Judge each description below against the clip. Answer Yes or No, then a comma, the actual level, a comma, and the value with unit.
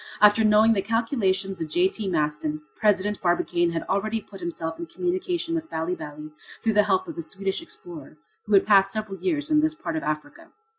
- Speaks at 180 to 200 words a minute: Yes, average, 195 wpm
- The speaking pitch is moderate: No, high, 195 Hz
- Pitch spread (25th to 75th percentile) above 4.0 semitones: Yes, average, 4.8 semitones